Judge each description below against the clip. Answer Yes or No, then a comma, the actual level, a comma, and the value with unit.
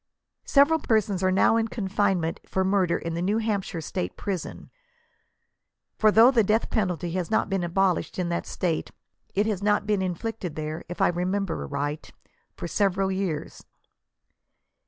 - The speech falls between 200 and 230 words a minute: No, average, 160 wpm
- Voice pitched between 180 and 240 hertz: Yes, high, 190 Hz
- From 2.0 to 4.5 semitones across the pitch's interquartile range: Yes, average, 3.4 semitones